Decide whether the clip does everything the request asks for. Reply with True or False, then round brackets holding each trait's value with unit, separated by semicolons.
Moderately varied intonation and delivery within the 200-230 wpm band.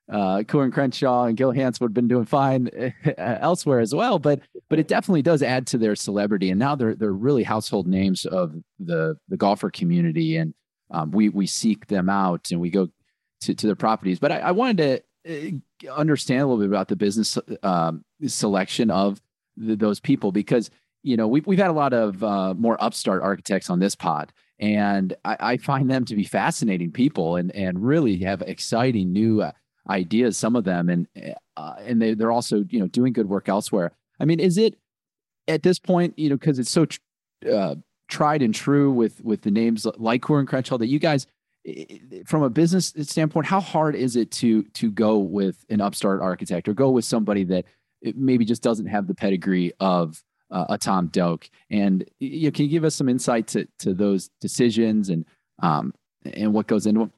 False (6.4 semitones; 205 wpm)